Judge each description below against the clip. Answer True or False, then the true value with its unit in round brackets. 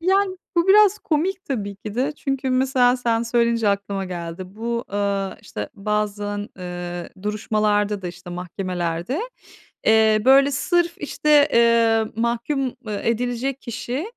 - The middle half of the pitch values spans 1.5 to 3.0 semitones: False (5.1 semitones)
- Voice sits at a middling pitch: False (230 Hz)